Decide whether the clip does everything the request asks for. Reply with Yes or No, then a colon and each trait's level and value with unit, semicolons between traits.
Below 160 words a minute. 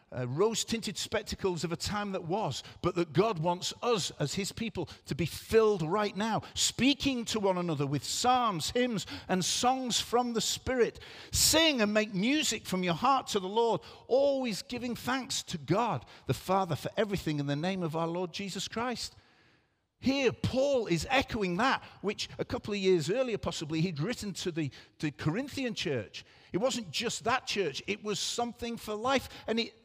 No: average, 190 wpm